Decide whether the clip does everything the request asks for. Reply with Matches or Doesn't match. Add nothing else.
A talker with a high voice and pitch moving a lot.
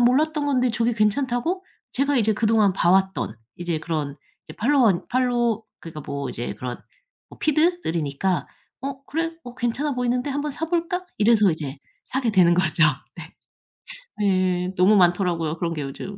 Matches